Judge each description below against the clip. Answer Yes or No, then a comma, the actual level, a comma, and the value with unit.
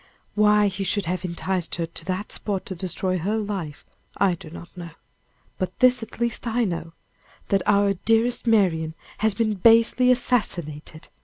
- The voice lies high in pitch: Yes, high, 195 Hz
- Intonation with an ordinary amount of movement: Yes, average, 4.3 semitones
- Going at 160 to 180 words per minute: Yes, average, 165 wpm